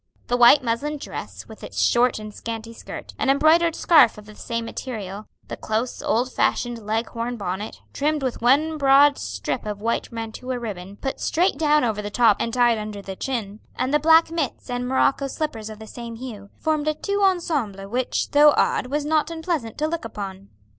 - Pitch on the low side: No, high, 245 Hz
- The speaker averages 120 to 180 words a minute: No, average, 195 wpm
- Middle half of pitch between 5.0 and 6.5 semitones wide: Yes, average, 5.3 semitones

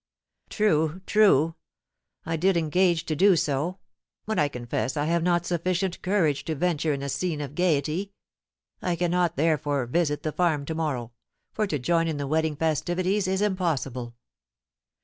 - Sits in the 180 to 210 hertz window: No, medium, 165 Hz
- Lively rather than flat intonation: No, average, 3.6 semitones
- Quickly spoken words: No, average, 160 wpm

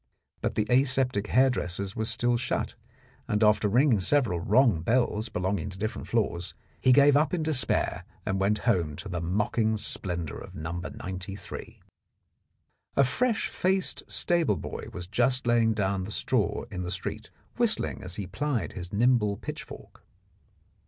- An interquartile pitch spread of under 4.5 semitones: No, average, 5.3 semitones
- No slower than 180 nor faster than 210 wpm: No, average, 150 wpm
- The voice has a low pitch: Yes, low, 105 Hz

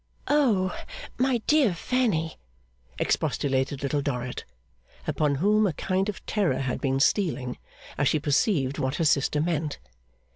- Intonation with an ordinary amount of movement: No, wide, 6.7 semitones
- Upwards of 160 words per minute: No, slow, 135 wpm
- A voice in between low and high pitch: Yes, medium, 155 Hz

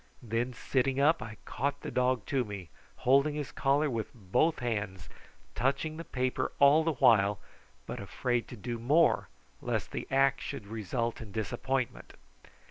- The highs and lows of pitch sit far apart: No, average, 3.7 semitones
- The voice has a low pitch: Yes, low, 125 Hz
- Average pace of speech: Yes, average, 155 wpm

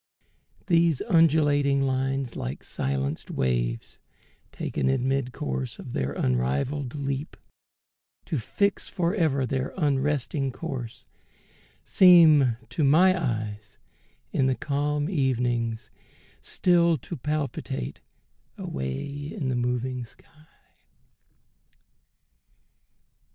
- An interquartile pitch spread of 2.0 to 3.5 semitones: No, average, 4.7 semitones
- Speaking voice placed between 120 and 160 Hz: Yes, low, 135 Hz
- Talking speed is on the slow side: Yes, slow, 95 wpm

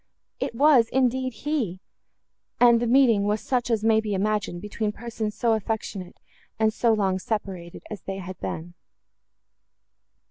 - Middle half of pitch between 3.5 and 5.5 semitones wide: No, average, 2.9 semitones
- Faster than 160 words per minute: No, average, 145 wpm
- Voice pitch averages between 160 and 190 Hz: No, high, 220 Hz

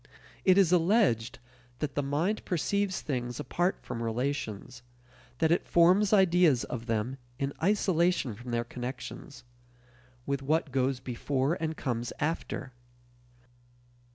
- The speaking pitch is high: No, medium, 140 Hz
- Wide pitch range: Yes, wide, 6.0 semitones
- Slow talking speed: Yes, slow, 125 wpm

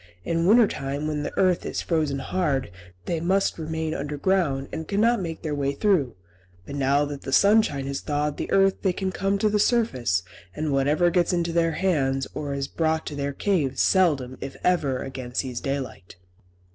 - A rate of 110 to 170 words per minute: No, average, 185 wpm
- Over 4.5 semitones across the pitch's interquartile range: Yes, average, 4.9 semitones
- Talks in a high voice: No, medium, 155 Hz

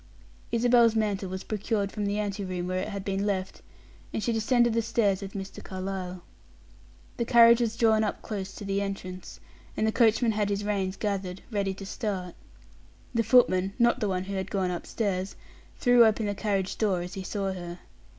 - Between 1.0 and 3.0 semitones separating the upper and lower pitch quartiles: Yes, narrow, 2.6 semitones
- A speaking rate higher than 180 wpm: Yes, average, 190 wpm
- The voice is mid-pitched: No, high, 200 Hz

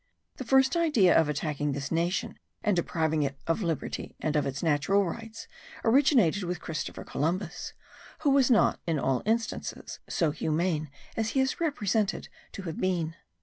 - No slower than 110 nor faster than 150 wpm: No, average, 160 wpm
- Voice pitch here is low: No, medium, 175 Hz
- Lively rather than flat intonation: Yes, wide, 6.3 semitones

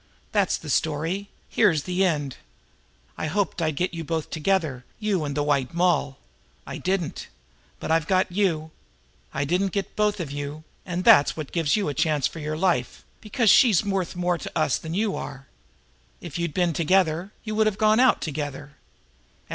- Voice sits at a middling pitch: Yes, medium, 170 Hz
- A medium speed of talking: Yes, average, 180 wpm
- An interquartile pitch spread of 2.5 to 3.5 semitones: No, average, 4.3 semitones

